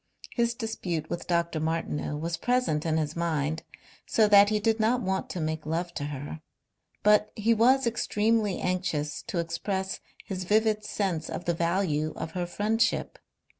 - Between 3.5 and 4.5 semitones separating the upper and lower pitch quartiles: No, average, 5.1 semitones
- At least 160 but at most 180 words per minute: Yes, average, 165 wpm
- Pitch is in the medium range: Yes, medium, 180 Hz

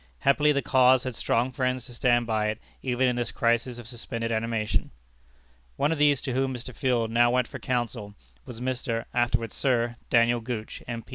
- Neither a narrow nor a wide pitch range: No, narrow, 1.8 semitones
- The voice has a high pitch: No, low, 120 Hz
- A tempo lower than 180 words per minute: No, average, 190 wpm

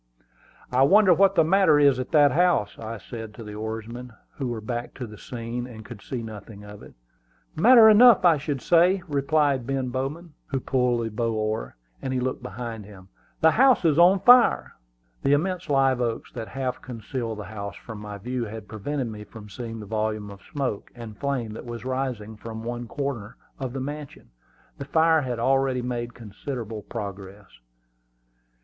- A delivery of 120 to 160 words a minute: No, average, 185 wpm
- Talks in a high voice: No, low, 125 Hz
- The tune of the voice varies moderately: Yes, average, 4.5 semitones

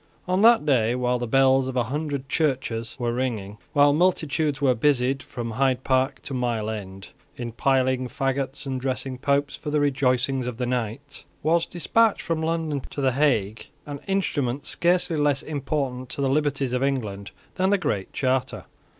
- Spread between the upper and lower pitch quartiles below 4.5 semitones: Yes, average, 2.9 semitones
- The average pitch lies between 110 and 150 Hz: Yes, low, 135 Hz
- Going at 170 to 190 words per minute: Yes, average, 175 wpm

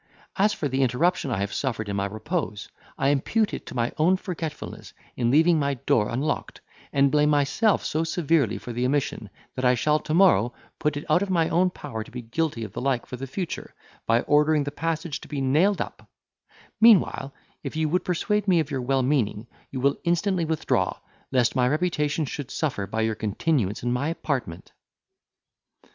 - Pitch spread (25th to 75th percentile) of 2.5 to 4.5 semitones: No, average, 4.9 semitones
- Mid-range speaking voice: Yes, medium, 145 Hz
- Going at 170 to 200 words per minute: Yes, average, 195 wpm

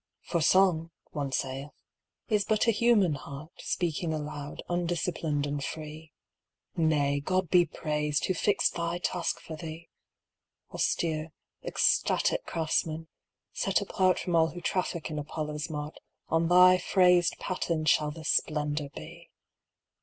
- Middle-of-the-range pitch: Yes, medium, 160 Hz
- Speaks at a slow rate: Yes, slow, 130 wpm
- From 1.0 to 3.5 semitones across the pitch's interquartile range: Yes, average, 3.0 semitones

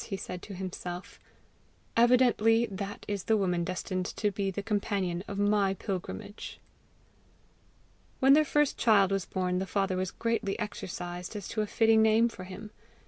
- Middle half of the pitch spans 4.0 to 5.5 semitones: No, average, 3.0 semitones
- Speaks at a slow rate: No, average, 160 wpm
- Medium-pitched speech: No, high, 200 Hz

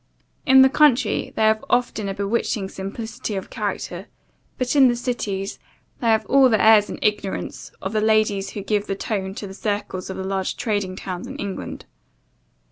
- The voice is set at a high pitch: Yes, high, 210 Hz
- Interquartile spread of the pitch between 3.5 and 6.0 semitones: No, average, 3.0 semitones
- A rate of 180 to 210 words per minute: Yes, average, 185 wpm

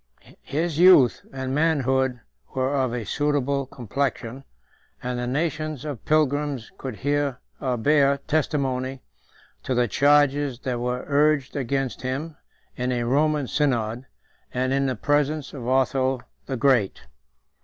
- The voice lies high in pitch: No, low, 135 Hz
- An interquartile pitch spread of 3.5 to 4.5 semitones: No, narrow, 2.5 semitones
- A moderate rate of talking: No, slow, 130 wpm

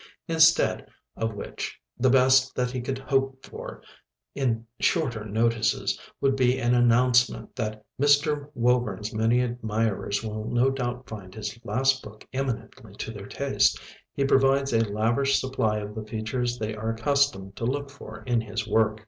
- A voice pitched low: Yes, low, 120 Hz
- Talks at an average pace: Yes, average, 155 wpm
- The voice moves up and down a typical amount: Yes, average, 3.4 semitones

